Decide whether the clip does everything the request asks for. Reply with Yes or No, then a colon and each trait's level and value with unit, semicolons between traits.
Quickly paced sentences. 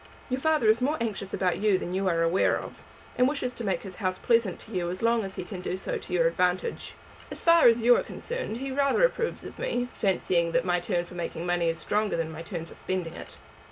Yes: fast, 250 wpm